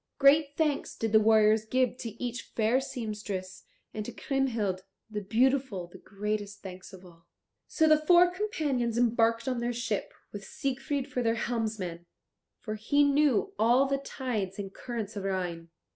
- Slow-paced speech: No, average, 160 wpm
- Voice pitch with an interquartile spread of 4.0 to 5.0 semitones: Yes, average, 4.7 semitones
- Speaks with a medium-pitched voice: No, high, 230 Hz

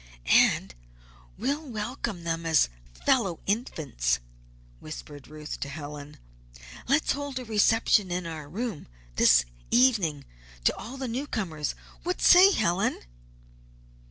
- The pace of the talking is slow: Yes, slow, 115 wpm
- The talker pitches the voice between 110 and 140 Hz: No, high, 195 Hz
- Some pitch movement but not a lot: No, wide, 8.4 semitones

